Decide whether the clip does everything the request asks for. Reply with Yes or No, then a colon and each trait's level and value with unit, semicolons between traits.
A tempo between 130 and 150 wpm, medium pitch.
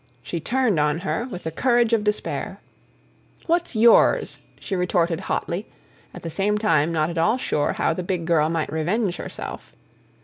No: average, 170 wpm; medium, 180 Hz